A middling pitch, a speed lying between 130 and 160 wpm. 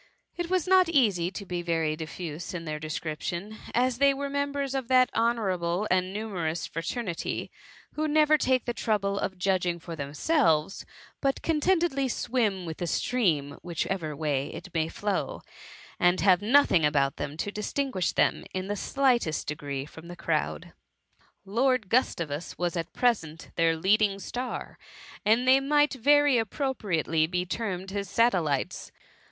No: high, 195 Hz; average, 155 wpm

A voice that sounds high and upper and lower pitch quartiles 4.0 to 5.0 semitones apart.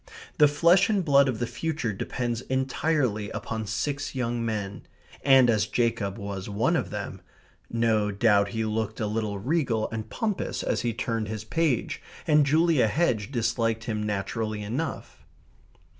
No: low, 115 Hz; average, 4.3 semitones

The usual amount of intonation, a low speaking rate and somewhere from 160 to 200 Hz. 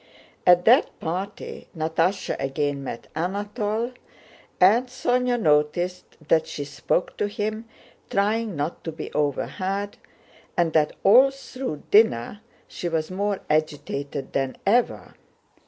No: wide, 5.8 semitones; slow, 120 wpm; medium, 185 Hz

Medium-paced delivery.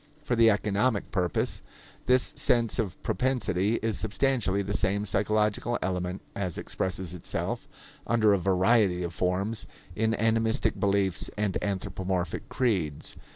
No: slow, 125 wpm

